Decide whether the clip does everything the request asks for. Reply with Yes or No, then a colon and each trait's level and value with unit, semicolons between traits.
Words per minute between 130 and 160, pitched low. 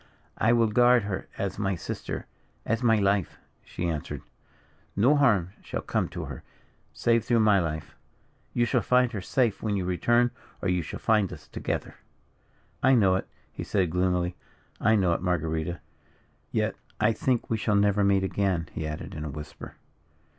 No: average, 175 wpm; low, 100 Hz